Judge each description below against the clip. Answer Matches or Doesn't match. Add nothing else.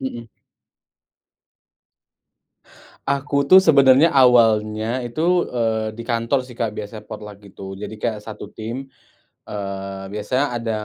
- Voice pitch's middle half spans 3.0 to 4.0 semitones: Matches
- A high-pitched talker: Doesn't match